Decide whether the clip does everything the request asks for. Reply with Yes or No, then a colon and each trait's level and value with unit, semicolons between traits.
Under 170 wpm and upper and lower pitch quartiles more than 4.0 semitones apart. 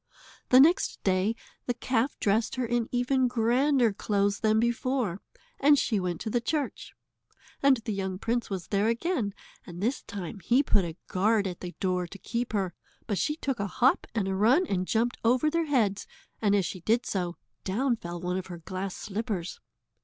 No: average, 190 wpm; average, 4.5 semitones